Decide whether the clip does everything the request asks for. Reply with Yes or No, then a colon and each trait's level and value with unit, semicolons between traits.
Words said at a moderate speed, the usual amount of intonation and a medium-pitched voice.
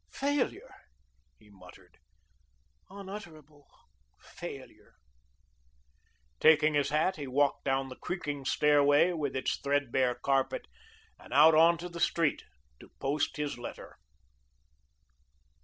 No: slow, 105 wpm; average, 3.5 semitones; medium, 145 Hz